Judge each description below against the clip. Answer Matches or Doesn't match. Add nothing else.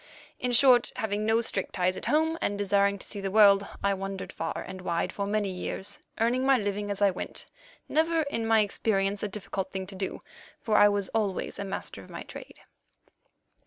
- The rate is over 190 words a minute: Matches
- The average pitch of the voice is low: Doesn't match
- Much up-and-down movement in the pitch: Doesn't match